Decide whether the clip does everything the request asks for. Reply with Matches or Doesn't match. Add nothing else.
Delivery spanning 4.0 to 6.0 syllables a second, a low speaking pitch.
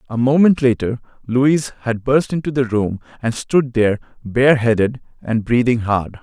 Matches